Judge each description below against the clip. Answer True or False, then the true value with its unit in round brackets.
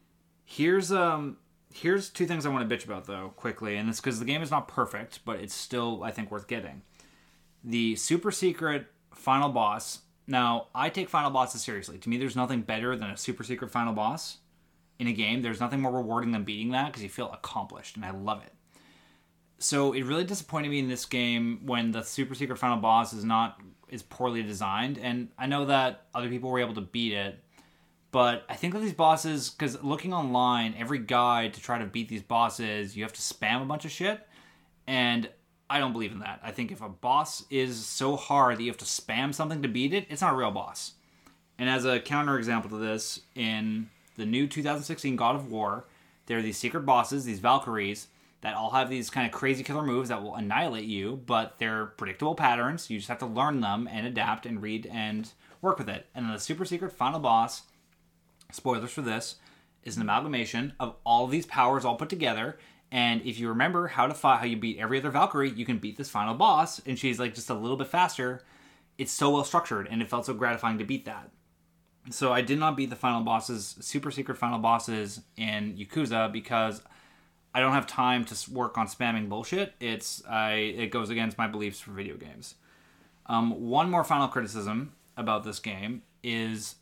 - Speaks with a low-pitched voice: True (120 Hz)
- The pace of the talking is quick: True (210 wpm)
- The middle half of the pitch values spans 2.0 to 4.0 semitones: True (3.5 semitones)